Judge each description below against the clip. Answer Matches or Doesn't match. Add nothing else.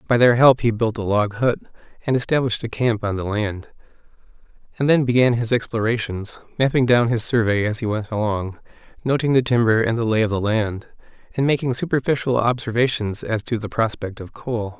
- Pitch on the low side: Matches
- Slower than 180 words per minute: Doesn't match